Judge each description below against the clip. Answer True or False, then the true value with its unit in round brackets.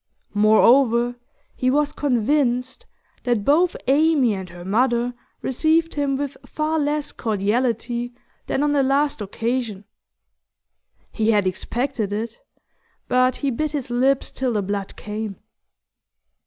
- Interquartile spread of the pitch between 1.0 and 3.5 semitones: False (4.5 semitones)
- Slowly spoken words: True (125 wpm)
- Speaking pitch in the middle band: False (245 Hz)